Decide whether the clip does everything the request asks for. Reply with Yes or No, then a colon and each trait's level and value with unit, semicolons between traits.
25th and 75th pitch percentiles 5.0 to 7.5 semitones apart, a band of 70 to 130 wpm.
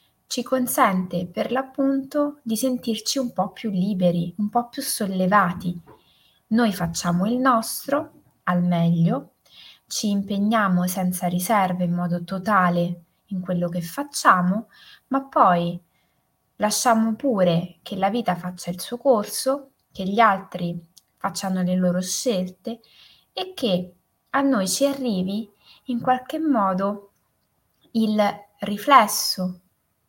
Yes: wide, 5.5 semitones; average, 120 wpm